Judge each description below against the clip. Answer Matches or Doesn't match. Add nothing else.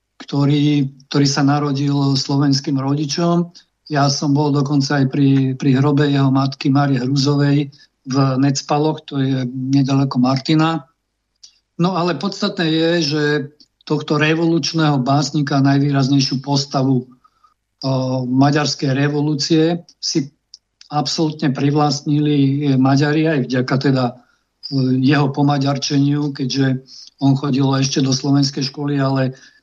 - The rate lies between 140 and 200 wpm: Doesn't match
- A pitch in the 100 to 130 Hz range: Doesn't match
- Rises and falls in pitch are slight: Matches